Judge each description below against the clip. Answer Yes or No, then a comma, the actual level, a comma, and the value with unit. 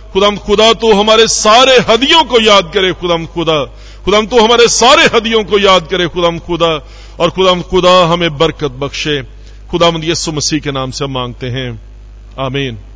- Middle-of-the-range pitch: Yes, medium, 170 Hz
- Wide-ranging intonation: Yes, wide, 7.2 semitones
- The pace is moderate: Yes, average, 175 wpm